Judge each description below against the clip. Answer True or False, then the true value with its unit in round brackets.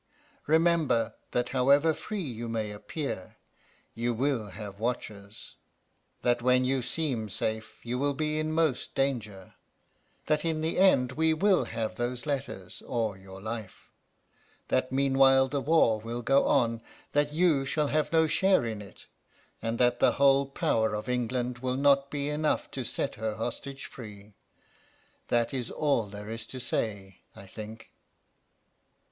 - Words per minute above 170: False (150 wpm)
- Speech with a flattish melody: False (4.4 semitones)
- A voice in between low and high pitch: False (125 Hz)